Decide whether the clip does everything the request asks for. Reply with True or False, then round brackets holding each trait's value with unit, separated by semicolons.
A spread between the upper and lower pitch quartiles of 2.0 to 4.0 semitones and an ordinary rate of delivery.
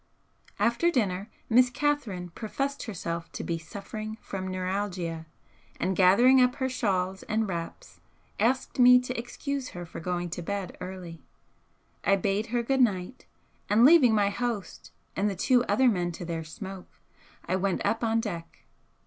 False (5.2 semitones; 155 wpm)